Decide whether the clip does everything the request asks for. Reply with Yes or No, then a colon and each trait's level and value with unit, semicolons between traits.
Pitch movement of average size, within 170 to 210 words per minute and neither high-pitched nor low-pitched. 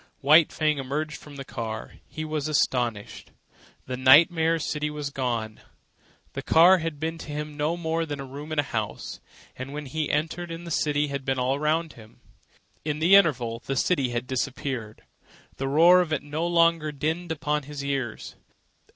Yes: average, 3.2 semitones; average, 185 wpm; medium, 150 Hz